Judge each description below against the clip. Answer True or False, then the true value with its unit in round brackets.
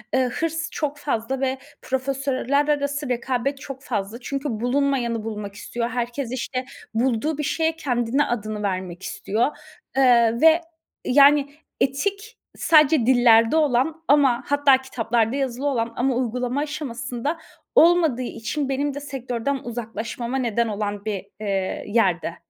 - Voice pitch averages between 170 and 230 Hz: False (255 Hz)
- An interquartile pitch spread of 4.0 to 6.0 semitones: False (3.5 semitones)